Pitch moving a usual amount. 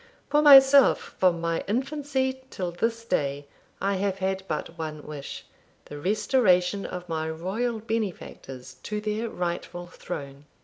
No: wide, 5.8 semitones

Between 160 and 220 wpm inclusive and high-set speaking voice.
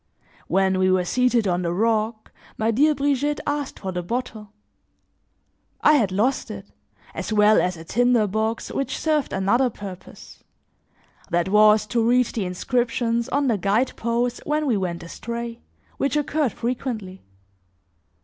No: average, 150 wpm; high, 230 Hz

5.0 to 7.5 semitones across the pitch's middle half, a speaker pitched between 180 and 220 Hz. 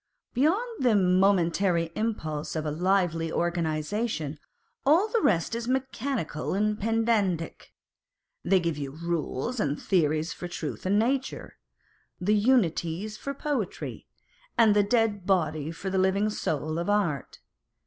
Yes: wide, 5.4 semitones; high, 190 Hz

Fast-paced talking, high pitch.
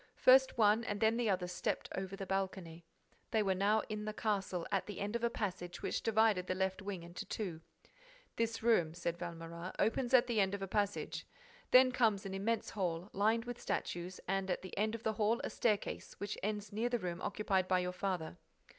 Yes: fast, 210 wpm; high, 200 Hz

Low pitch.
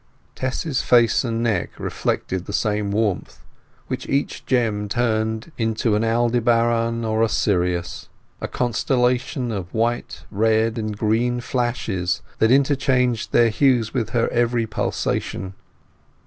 Yes: low, 115 Hz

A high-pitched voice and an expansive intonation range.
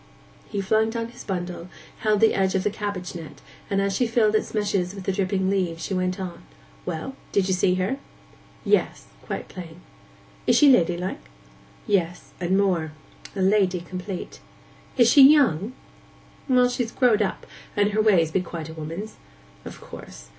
No: high, 195 Hz; average, 3.1 semitones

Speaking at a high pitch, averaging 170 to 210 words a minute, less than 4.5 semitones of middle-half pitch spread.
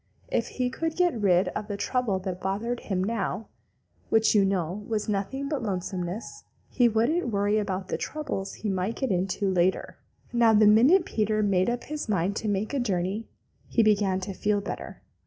Yes: high, 210 Hz; average, 185 wpm; average, 3.5 semitones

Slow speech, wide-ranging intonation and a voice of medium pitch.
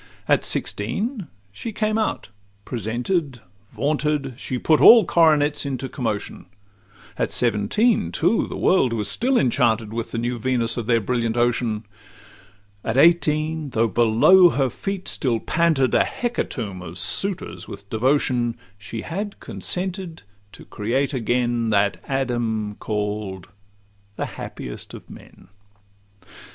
No: slow, 125 wpm; wide, 6.1 semitones; low, 125 Hz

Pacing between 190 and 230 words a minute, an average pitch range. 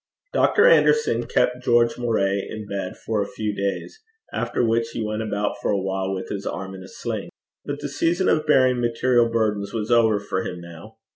Yes: average, 200 wpm; average, 3.3 semitones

